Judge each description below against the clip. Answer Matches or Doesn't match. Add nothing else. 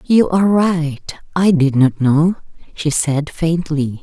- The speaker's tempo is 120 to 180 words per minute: Matches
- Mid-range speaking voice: Matches